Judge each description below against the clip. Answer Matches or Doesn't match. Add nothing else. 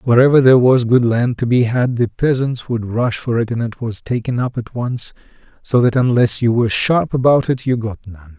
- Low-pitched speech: Matches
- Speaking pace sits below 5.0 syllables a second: Doesn't match